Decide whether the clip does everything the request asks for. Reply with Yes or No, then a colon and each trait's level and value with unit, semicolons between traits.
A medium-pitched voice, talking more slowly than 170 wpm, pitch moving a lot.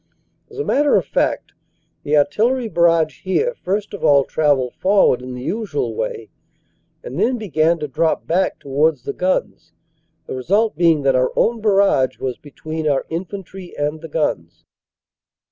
Yes: medium, 165 Hz; average, 160 wpm; wide, 6.2 semitones